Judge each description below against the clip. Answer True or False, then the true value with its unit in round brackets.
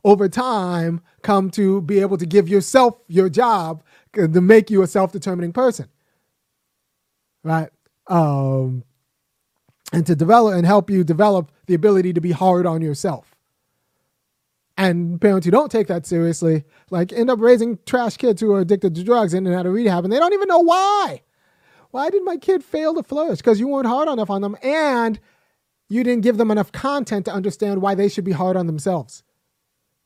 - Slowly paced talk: False (180 wpm)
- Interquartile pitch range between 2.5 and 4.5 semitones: False (5.0 semitones)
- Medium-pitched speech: False (200 Hz)